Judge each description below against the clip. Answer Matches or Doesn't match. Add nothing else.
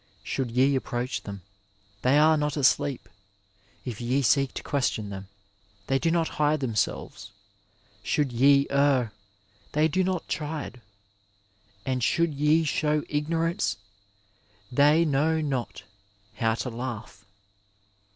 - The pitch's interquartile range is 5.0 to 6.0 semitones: Doesn't match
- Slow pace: Matches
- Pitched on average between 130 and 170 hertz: Matches